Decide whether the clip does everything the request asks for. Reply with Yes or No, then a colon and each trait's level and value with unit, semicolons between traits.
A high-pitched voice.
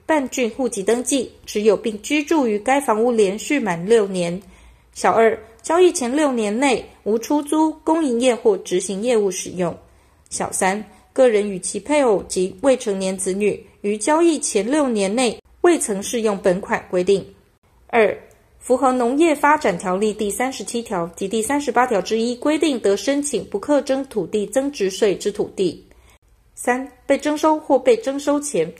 Yes: high, 240 Hz